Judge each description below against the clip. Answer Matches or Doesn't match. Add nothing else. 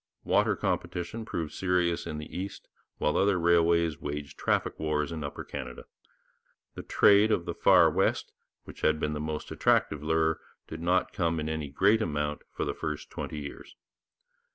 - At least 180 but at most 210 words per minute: Doesn't match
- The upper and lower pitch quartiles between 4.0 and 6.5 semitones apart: Doesn't match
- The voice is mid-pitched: Doesn't match